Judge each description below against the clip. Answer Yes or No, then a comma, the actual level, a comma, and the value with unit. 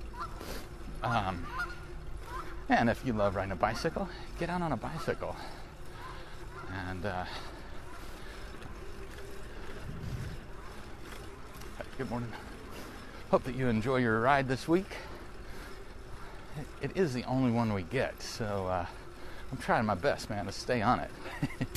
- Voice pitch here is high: No, low, 120 Hz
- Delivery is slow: Yes, slow, 120 wpm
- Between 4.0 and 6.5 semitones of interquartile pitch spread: Yes, average, 4.5 semitones